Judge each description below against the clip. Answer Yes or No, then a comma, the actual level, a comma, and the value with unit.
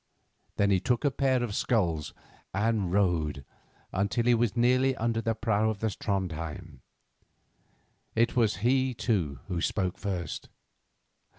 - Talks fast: No, slow, 135 wpm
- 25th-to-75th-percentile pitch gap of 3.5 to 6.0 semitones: Yes, average, 4.4 semitones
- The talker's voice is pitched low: Yes, low, 105 Hz